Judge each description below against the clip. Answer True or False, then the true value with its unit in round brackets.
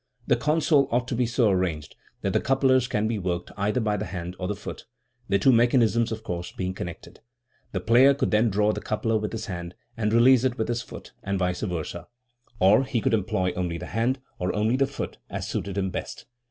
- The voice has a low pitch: True (110 Hz)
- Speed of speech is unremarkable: False (220 wpm)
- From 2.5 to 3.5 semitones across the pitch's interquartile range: False (4.4 semitones)